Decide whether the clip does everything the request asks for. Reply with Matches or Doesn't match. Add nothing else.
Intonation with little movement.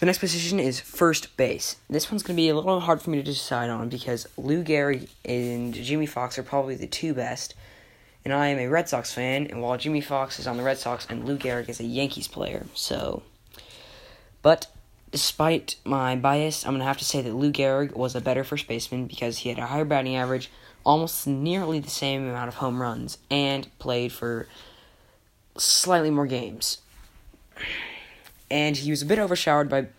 Doesn't match